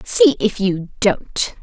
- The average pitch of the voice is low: No, high, 205 Hz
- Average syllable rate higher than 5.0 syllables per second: No, 3.0 syllables/s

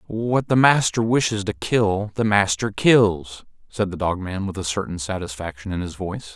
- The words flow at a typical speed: Yes, average, 190 wpm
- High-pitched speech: No, low, 100 Hz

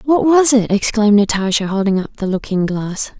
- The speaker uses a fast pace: No, average, 190 wpm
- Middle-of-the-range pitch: No, high, 215 Hz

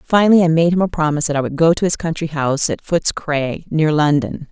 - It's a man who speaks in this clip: No, female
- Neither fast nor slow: No, fast, 255 wpm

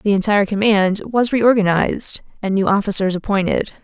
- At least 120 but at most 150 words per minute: Yes, average, 140 wpm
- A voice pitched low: No, high, 205 Hz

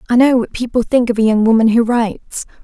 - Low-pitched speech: No, high, 230 Hz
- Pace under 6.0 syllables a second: No, 6.1 syllables/s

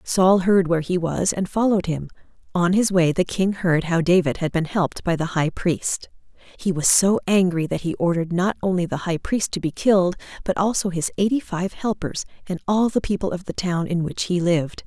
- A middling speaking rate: No, fast, 220 wpm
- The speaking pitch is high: No, medium, 180 Hz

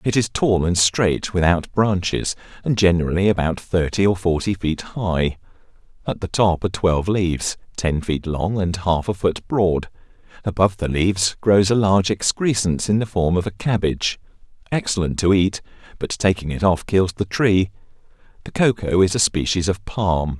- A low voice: Yes, very low, 95 Hz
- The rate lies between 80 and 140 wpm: No, average, 175 wpm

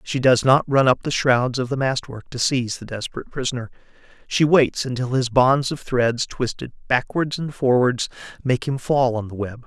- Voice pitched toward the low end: Yes, low, 125 Hz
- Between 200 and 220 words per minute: Yes, fast, 205 wpm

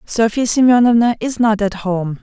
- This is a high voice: Yes, high, 220 Hz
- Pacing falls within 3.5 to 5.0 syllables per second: Yes, 4.8 syllables/s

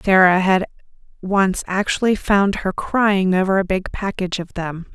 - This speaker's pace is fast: No, average, 160 wpm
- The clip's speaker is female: Yes, female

